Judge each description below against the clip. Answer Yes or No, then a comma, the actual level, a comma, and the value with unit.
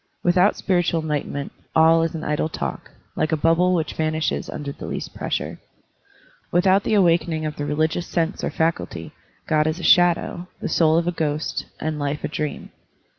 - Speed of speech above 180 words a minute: No, average, 175 wpm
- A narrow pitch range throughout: Yes, narrow, 2.2 semitones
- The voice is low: No, medium, 160 Hz